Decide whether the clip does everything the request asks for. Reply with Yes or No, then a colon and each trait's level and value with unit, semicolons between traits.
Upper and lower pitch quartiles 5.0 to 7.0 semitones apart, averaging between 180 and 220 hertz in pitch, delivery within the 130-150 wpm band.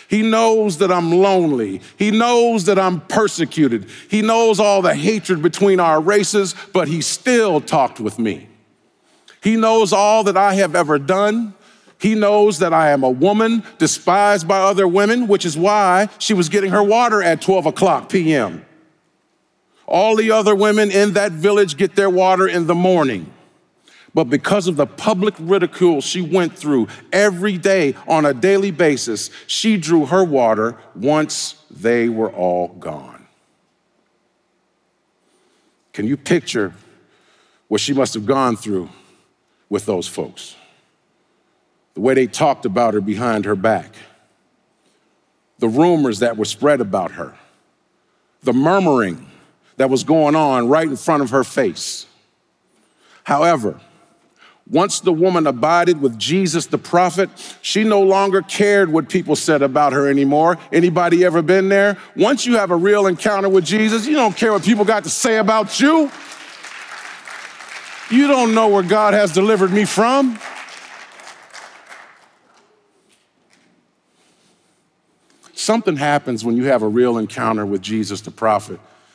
Yes: wide, 5.6 semitones; high, 190 Hz; average, 145 wpm